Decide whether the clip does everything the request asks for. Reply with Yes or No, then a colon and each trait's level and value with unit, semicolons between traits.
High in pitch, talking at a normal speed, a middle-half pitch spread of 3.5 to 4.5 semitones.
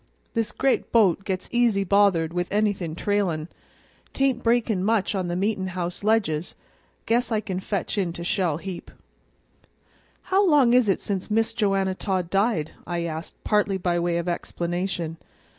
Yes: high, 195 Hz; average, 160 wpm; average, 3.8 semitones